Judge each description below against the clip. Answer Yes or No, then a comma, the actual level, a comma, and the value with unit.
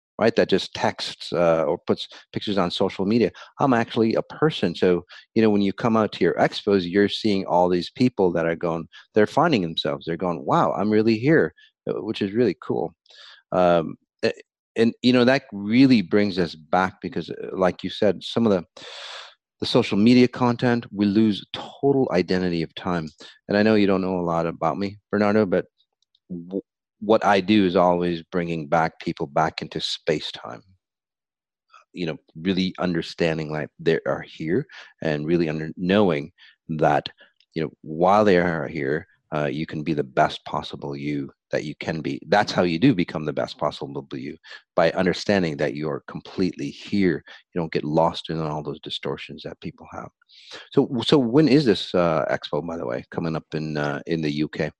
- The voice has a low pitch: Yes, very low, 95 Hz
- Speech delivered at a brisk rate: No, average, 190 wpm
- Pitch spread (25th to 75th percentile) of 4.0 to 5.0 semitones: Yes, average, 4.4 semitones